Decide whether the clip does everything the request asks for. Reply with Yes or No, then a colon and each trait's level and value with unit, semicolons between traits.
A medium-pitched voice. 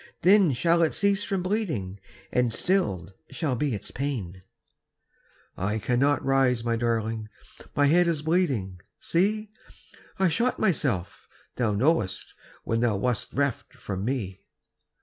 No: low, 130 Hz